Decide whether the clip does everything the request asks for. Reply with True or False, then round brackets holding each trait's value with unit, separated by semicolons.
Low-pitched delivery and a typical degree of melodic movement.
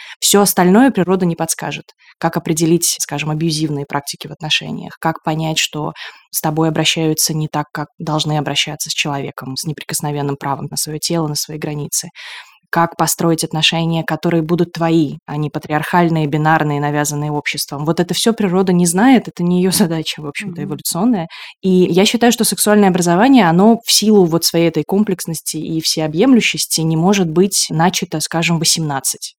False (165 Hz; 3.0 semitones)